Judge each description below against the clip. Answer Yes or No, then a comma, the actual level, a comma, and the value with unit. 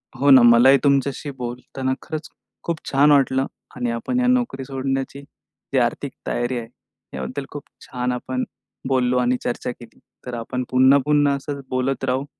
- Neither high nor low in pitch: No, low, 130 Hz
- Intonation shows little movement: Yes, narrow, 2.0 semitones